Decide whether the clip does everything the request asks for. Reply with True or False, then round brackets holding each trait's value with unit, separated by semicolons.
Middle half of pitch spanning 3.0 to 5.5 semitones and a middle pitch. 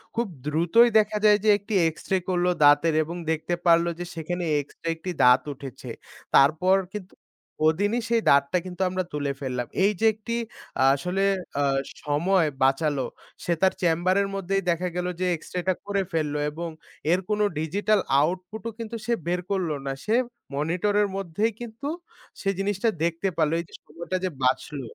True (4.2 semitones; 180 Hz)